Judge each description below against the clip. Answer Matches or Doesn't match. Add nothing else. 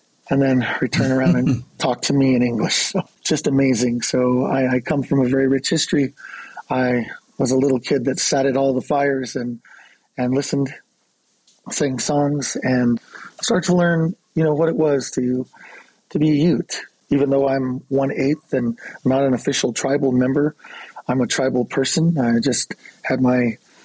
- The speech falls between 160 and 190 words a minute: Matches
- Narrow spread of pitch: Matches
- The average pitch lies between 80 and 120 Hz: Doesn't match